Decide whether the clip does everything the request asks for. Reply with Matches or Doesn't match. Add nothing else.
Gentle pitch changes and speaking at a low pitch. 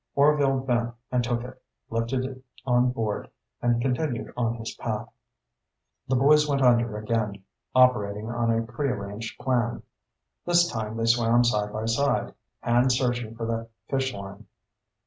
Matches